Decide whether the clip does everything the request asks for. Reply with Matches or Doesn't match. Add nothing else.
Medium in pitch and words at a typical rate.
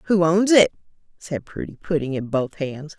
Matches